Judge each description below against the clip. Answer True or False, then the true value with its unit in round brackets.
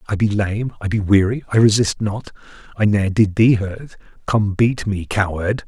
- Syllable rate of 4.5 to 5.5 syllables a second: True (4.7 syllables/s)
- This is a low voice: True (105 Hz)